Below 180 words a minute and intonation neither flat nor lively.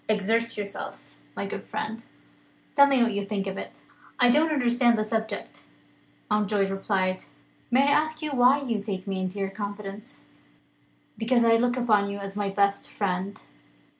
Yes: average, 165 wpm; average, 3.3 semitones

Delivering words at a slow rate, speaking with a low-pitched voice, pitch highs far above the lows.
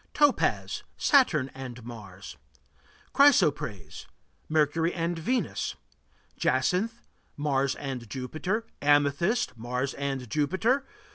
No: slow, 85 wpm; medium, 145 Hz; wide, 6.0 semitones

